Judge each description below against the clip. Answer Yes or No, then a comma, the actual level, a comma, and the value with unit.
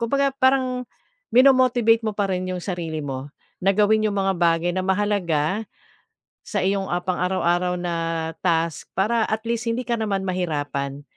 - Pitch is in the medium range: No, high, 195 Hz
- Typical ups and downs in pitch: Yes, average, 4.5 semitones